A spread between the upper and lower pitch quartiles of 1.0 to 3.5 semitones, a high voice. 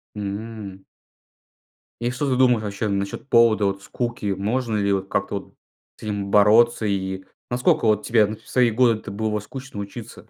No: average, 3.0 semitones; low, 105 Hz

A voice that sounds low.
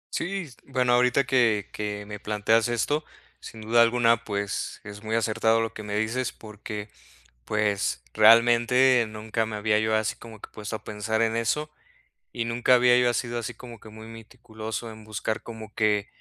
Yes: low, 110 Hz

